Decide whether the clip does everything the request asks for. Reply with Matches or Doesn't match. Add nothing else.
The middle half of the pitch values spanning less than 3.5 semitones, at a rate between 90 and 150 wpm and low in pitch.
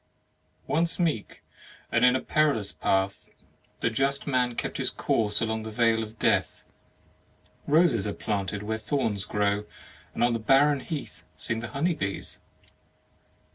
Doesn't match